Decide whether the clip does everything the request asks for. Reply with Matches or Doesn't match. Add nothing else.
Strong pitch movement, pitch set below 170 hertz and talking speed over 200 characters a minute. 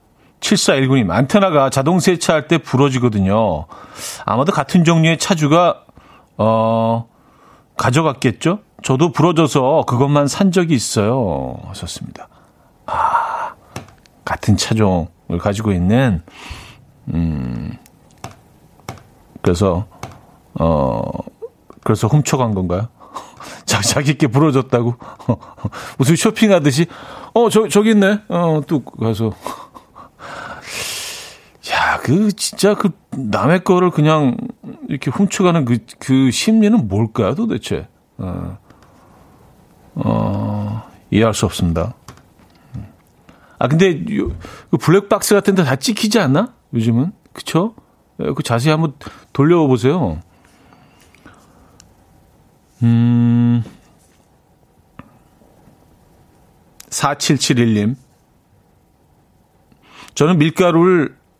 Doesn't match